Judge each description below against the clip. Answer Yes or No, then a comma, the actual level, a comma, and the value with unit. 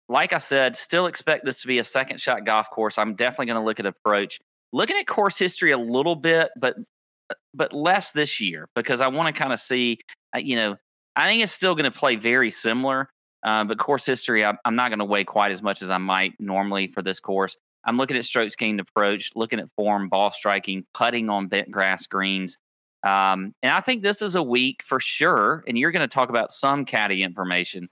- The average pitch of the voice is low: Yes, low, 115 Hz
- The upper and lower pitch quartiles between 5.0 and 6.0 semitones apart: Yes, wide, 5.4 semitones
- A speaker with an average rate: No, fast, 220 wpm